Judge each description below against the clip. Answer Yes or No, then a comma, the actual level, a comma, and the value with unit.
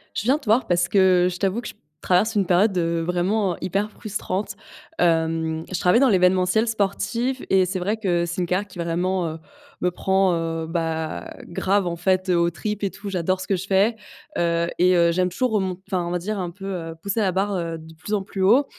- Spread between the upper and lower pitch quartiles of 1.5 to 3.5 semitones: Yes, average, 2.8 semitones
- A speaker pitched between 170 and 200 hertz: Yes, medium, 185 Hz